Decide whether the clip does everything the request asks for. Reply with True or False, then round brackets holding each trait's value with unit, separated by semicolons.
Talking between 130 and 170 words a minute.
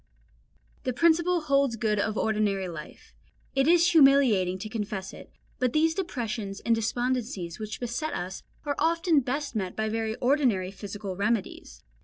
True (150 wpm)